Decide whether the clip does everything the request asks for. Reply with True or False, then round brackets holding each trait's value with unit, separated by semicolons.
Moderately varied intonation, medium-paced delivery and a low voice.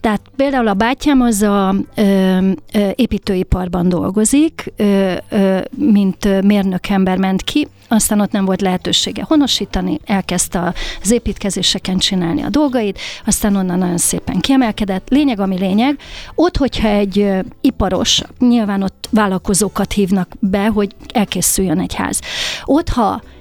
False (3.1 semitones; 135 wpm; 200 Hz)